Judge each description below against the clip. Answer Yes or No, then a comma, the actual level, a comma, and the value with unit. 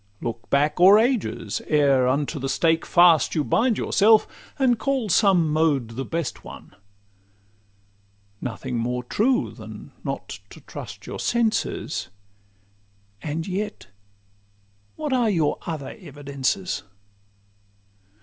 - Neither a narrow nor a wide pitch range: No, wide, 7.4 semitones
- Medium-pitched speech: Yes, medium, 165 Hz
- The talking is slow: Yes, slow, 115 wpm